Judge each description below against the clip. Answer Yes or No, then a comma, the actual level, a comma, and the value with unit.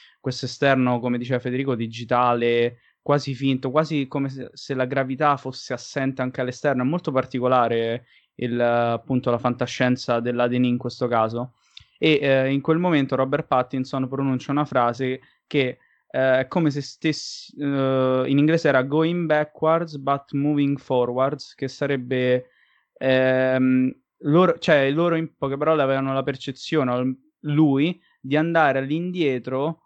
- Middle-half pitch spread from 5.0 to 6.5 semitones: No, narrow, 2.5 semitones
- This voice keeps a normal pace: Yes, average, 140 wpm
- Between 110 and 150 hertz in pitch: Yes, low, 135 Hz